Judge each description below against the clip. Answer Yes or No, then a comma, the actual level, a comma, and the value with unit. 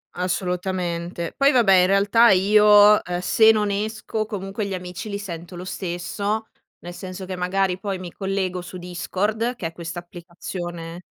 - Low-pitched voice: No, medium, 185 Hz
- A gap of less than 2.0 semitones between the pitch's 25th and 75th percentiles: No, average, 2.7 semitones